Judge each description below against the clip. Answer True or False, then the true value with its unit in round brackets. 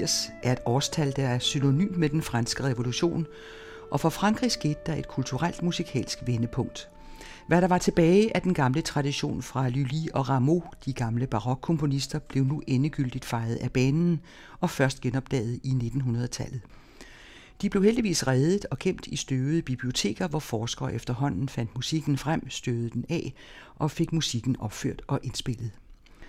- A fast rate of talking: False (160 wpm)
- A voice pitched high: False (135 Hz)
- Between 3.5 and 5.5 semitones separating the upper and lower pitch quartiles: True (4.3 semitones)